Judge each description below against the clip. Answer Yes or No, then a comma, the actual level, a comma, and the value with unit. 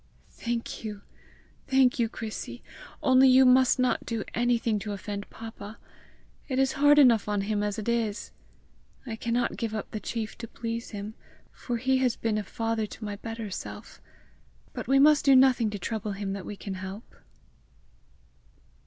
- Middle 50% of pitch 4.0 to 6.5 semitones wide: No, average, 3.2 semitones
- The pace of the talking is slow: No, average, 170 wpm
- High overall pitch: Yes, high, 225 Hz